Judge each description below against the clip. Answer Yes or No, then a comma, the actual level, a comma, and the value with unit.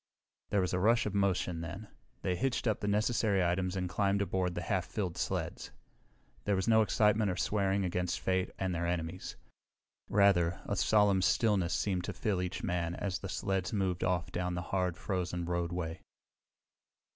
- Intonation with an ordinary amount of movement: No, narrow, 2.3 semitones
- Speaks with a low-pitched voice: Yes, very low, 95 Hz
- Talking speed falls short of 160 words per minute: No, average, 175 wpm